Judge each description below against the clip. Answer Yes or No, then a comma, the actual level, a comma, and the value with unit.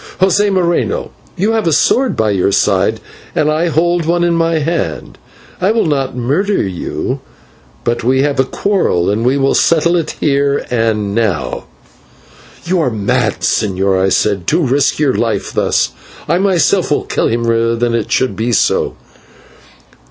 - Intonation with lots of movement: Yes, wide, 7.2 semitones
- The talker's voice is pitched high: No, medium, 140 Hz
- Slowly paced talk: No, average, 165 wpm